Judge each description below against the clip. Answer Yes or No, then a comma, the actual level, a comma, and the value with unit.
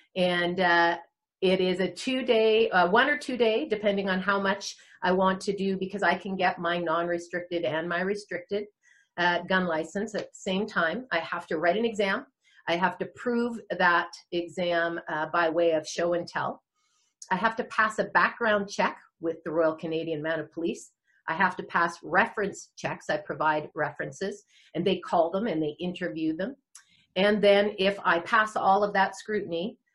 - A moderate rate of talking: Yes, average, 190 wpm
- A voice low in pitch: No, medium, 185 Hz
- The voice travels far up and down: No, average, 3.2 semitones